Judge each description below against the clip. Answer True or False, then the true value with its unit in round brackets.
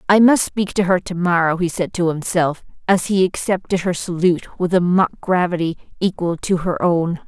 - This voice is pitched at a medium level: True (180 Hz)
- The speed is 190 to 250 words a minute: True (200 wpm)